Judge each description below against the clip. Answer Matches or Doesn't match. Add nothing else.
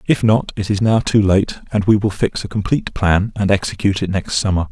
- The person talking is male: Matches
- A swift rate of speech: Matches